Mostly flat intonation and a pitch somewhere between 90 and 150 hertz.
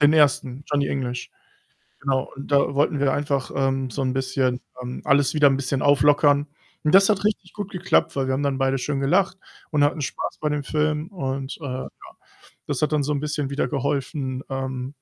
Yes: narrow, 2.0 semitones; medium, 140 Hz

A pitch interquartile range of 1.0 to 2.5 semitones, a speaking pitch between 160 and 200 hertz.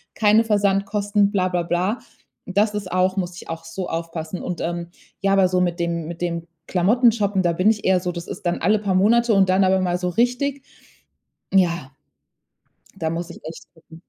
No: average, 2.9 semitones; medium, 185 Hz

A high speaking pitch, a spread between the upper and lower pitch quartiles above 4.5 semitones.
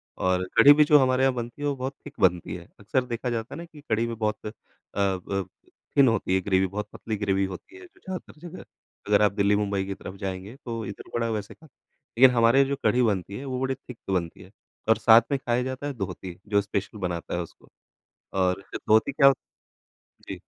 No: low, 110 Hz; average, 5.0 semitones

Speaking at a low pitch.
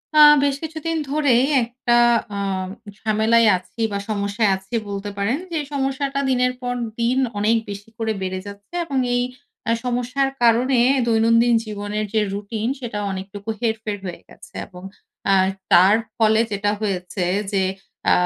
No: high, 225 Hz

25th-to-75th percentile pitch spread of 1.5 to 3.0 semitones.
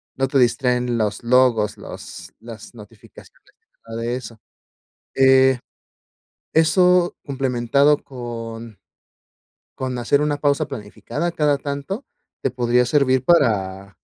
No: average, 3.5 semitones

